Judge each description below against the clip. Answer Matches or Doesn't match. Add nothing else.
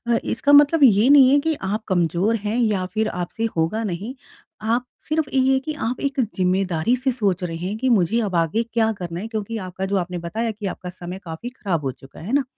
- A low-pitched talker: Doesn't match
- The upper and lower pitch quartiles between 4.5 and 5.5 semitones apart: Matches